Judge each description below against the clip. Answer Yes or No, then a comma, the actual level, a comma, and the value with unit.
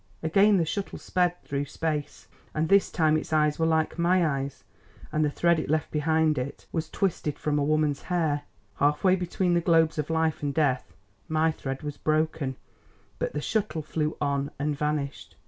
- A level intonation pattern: Yes, narrow, 1.9 semitones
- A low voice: No, medium, 155 Hz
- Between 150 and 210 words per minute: Yes, average, 185 wpm